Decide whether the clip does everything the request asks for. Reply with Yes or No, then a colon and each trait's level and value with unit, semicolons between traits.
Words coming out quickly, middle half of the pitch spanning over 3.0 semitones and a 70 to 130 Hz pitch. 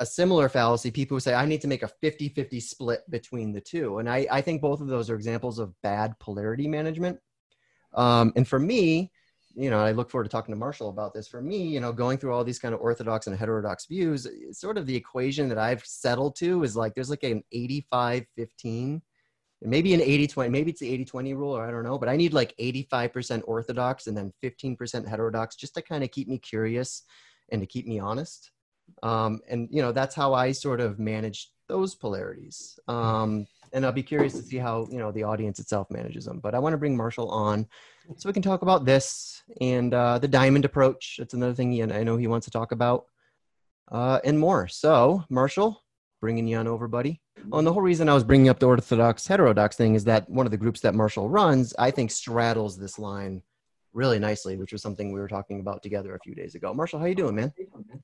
Yes: fast, 230 wpm; average, 3.7 semitones; low, 125 Hz